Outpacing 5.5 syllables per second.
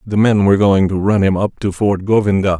Yes: 5.7 syllables/s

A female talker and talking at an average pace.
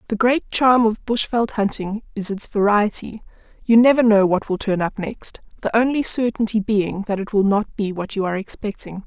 Yes: female; average, 190 wpm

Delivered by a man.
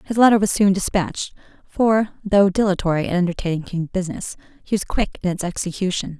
No: female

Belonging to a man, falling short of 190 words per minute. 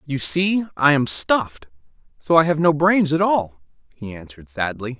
Yes: male; average, 180 wpm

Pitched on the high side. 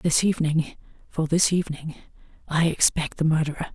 No: medium, 160 Hz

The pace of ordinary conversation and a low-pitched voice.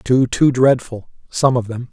Yes: average, 155 wpm; low, 125 Hz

